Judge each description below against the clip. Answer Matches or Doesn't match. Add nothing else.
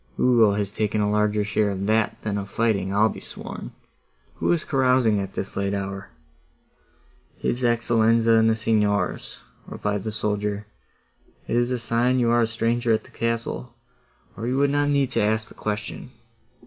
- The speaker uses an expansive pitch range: Doesn't match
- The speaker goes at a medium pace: Matches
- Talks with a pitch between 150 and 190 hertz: Doesn't match